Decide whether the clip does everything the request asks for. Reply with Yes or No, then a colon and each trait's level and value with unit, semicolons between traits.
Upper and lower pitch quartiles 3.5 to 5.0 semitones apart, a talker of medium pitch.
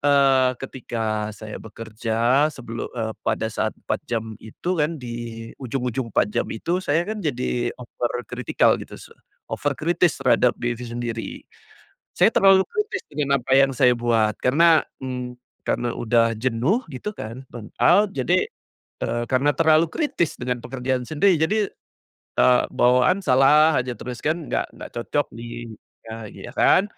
No: average, 4.4 semitones; low, 125 Hz